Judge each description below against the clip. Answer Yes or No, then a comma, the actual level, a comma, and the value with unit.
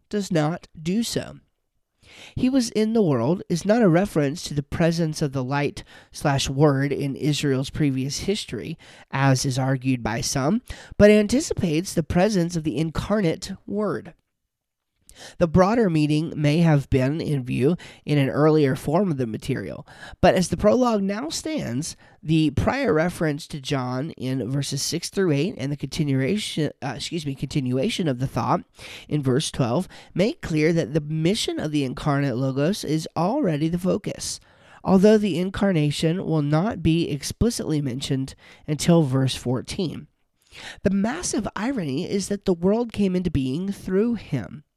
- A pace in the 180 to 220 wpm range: No, average, 160 wpm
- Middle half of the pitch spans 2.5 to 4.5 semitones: No, wide, 5.5 semitones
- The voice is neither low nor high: Yes, medium, 155 Hz